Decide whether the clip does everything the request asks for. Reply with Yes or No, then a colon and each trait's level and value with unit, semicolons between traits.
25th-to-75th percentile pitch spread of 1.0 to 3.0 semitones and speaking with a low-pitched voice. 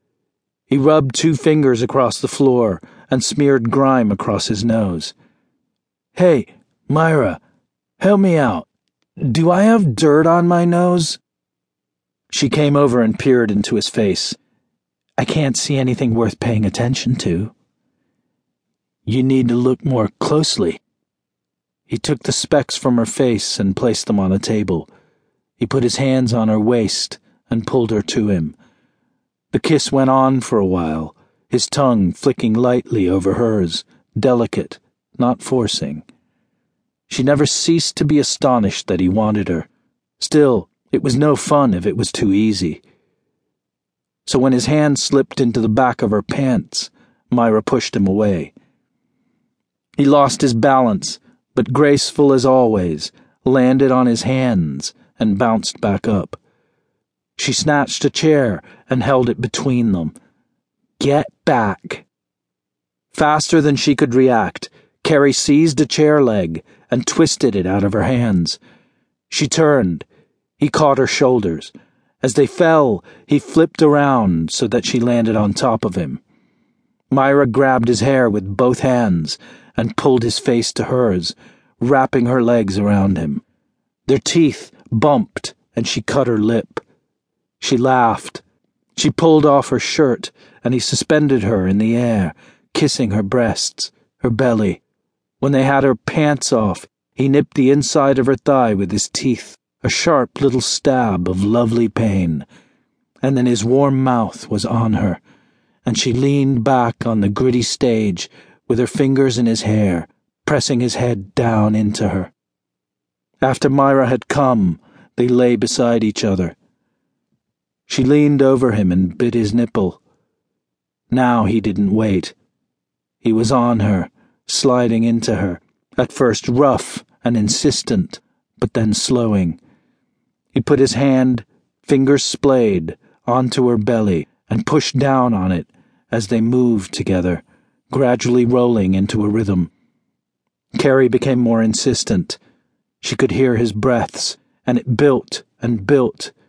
No: average, 4.1 semitones; low, 125 Hz